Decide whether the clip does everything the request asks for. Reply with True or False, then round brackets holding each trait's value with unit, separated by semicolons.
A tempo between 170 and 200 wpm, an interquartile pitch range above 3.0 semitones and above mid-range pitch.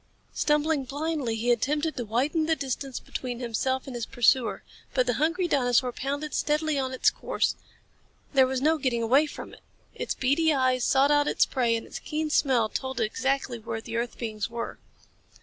True (185 wpm; 3.6 semitones; 260 Hz)